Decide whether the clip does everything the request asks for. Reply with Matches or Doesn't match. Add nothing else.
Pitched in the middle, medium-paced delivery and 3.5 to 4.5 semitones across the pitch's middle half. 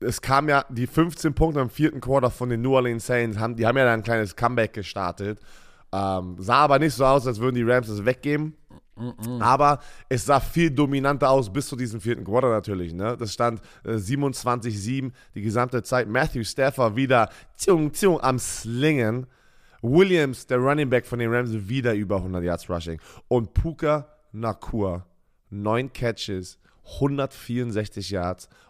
Doesn't match